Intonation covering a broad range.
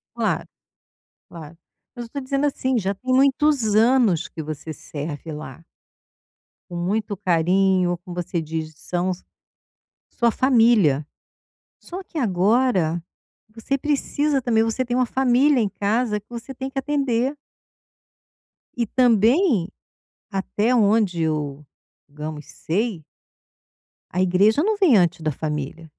Yes: wide, 7.3 semitones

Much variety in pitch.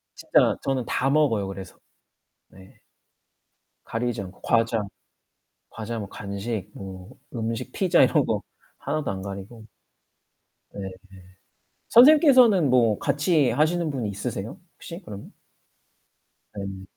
Yes: wide, 6.7 semitones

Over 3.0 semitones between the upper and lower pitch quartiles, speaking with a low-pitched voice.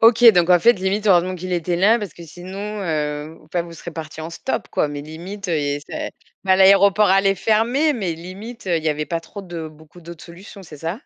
No: average, 3.4 semitones; medium, 180 Hz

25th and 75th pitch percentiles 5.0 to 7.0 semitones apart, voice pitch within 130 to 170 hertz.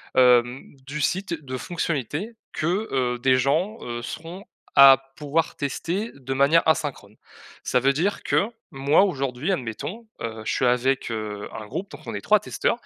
Yes: average, 5.3 semitones; medium, 140 Hz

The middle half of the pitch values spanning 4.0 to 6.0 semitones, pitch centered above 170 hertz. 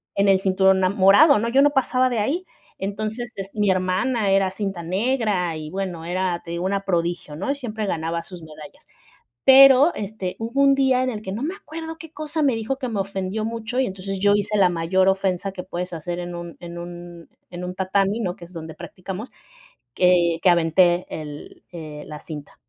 Yes: average, 4.5 semitones; high, 190 Hz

